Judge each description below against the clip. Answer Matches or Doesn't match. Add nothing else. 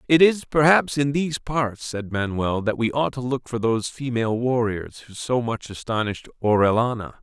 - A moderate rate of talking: Matches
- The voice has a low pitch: Matches